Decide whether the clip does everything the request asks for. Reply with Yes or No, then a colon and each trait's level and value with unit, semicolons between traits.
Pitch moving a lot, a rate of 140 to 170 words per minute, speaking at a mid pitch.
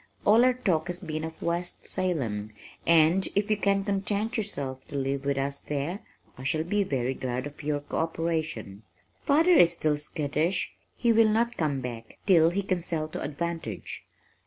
No: wide, 5.7 semitones; average, 180 wpm; medium, 160 Hz